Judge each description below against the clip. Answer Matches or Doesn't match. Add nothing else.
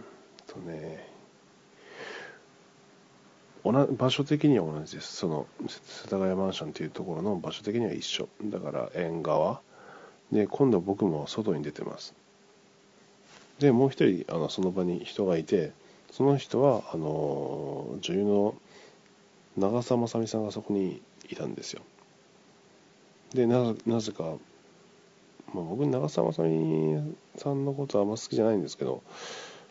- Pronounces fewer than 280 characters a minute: Matches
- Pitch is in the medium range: Doesn't match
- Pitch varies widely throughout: Matches